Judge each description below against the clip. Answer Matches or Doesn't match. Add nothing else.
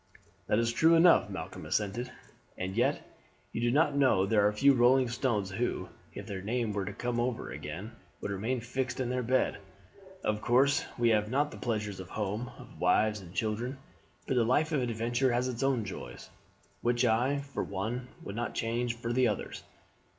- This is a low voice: Matches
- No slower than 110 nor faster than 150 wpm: Doesn't match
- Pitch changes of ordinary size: Matches